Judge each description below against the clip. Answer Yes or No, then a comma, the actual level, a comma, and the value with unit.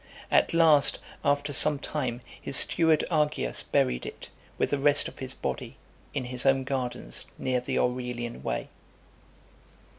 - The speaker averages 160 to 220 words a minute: No, average, 145 wpm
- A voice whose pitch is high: No, low, 135 Hz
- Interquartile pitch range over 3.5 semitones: No, average, 2.9 semitones